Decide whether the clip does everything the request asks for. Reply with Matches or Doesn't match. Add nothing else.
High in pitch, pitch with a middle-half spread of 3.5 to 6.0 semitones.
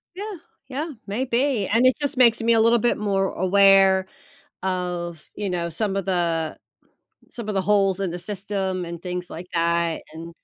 Matches